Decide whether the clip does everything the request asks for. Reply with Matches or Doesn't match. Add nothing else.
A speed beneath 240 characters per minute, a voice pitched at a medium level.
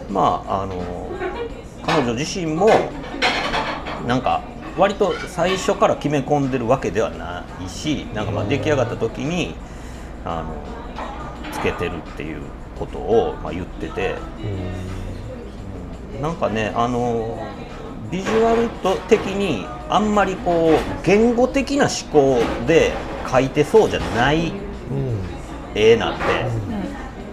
Doesn't match